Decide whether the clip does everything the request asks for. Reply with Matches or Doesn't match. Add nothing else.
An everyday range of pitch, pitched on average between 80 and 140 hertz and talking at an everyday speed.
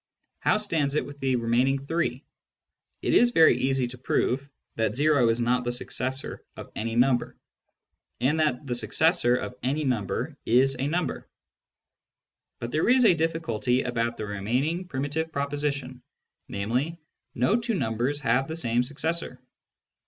Matches